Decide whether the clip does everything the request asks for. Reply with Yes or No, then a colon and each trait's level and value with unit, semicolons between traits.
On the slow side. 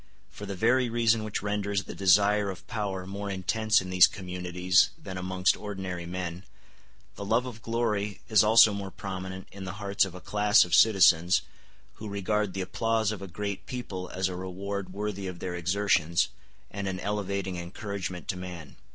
No: average, 175 wpm